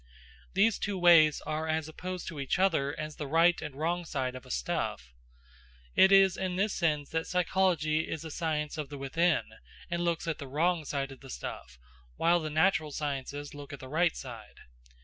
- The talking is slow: No, average, 195 wpm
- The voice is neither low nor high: Yes, medium, 155 Hz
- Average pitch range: Yes, average, 3.4 semitones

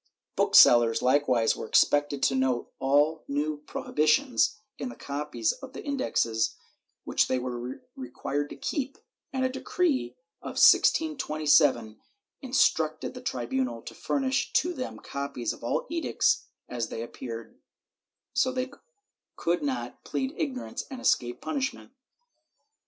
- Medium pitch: Yes, medium, 150 Hz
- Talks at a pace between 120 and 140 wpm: Yes, slow, 135 wpm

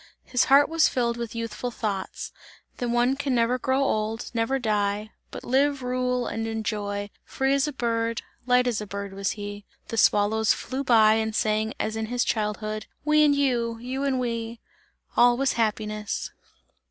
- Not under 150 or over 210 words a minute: Yes, average, 180 wpm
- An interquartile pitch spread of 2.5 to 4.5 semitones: Yes, average, 2.8 semitones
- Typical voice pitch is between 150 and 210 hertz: No, high, 230 Hz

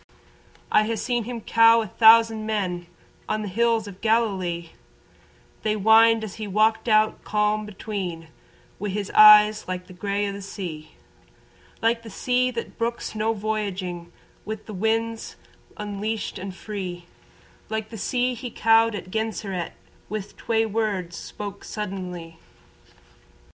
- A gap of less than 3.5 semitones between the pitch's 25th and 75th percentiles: Yes, narrow, 2.5 semitones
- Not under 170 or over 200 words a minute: No, average, 140 wpm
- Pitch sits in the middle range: No, high, 215 Hz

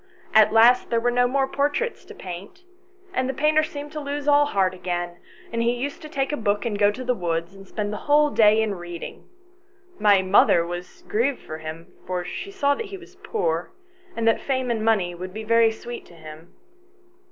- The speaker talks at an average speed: No, fast, 210 wpm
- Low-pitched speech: No, high, 225 Hz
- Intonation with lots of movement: Yes, wide, 7.3 semitones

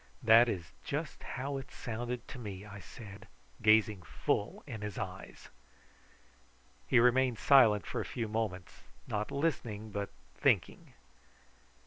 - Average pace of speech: No, slow, 130 wpm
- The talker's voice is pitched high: No, low, 110 Hz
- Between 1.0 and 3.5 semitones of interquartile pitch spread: Yes, average, 3.0 semitones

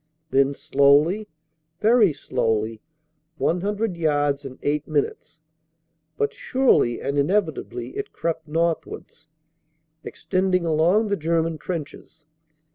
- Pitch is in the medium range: Yes, medium, 160 Hz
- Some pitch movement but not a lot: Yes, average, 4.7 semitones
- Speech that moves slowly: Yes, slow, 100 wpm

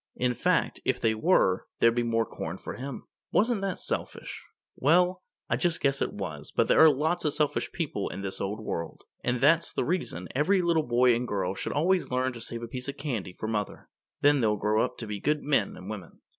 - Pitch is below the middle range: Yes, low, 125 Hz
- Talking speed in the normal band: No, fast, 225 wpm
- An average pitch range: No, wide, 6.3 semitones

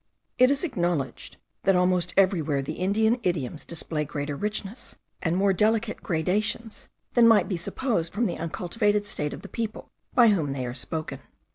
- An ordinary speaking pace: Yes, average, 165 wpm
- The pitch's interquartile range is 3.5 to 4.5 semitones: No, average, 5.3 semitones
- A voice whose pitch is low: No, medium, 185 Hz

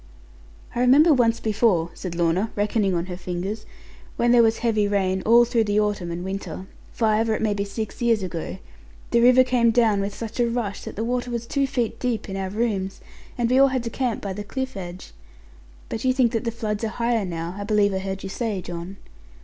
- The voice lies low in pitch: No, high, 215 Hz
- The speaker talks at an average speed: No, fast, 225 wpm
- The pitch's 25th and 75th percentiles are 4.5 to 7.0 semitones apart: No, average, 3.6 semitones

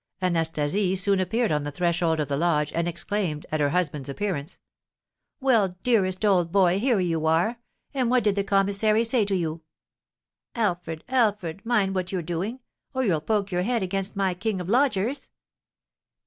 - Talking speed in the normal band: Yes, average, 170 wpm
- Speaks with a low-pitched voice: No, high, 190 Hz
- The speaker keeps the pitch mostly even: No, average, 4.0 semitones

